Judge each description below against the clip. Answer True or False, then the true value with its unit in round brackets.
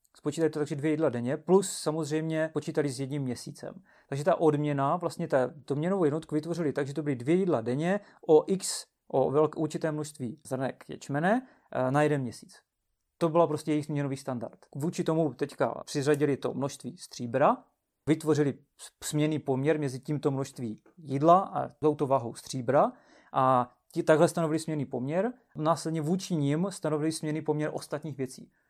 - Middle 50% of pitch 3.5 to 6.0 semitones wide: False (2.6 semitones)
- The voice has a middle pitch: True (150 Hz)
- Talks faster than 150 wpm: True (165 wpm)